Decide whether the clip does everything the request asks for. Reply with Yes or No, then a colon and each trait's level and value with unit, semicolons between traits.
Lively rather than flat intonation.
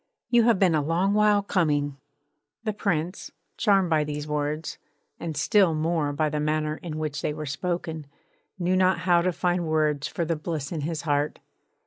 No: average, 3.2 semitones